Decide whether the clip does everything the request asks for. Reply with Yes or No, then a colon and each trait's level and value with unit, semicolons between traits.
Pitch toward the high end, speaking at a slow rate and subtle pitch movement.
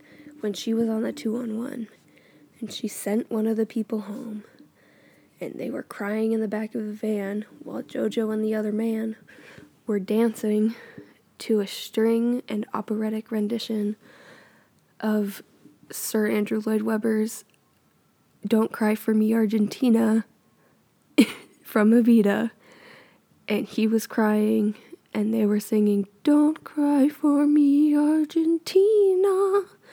Yes: high, 220 Hz; slow, 125 wpm; narrow, 1.9 semitones